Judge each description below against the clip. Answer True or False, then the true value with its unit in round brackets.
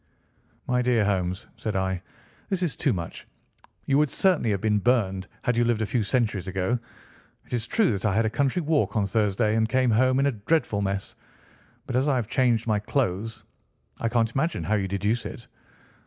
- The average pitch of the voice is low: True (115 Hz)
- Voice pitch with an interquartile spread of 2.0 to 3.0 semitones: False (4.0 semitones)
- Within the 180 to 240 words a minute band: True (200 wpm)